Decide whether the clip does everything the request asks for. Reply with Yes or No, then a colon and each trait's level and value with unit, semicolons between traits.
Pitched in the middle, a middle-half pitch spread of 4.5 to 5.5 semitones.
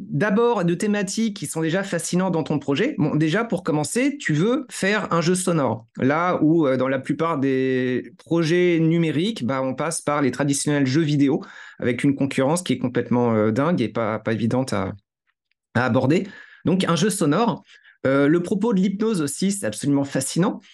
Yes: medium, 155 Hz; average, 5.2 semitones